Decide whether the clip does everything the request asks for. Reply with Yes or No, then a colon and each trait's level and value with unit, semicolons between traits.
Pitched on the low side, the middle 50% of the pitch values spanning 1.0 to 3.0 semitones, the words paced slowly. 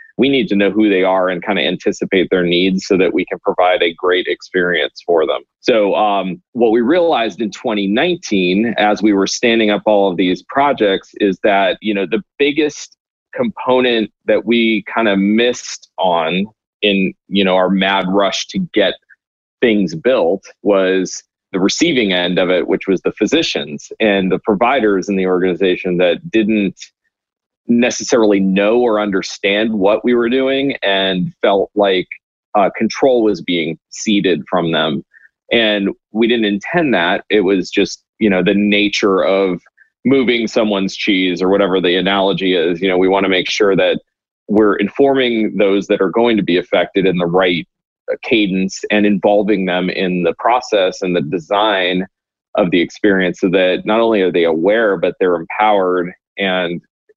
No: low, 100 Hz; average, 2.7 semitones; average, 170 wpm